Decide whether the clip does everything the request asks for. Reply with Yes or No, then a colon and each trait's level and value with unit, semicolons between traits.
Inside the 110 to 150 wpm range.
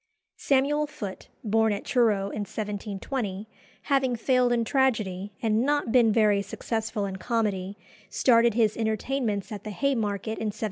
Yes: average, 145 wpm